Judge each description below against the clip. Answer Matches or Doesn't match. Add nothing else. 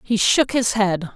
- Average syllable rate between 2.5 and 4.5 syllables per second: Matches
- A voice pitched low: Doesn't match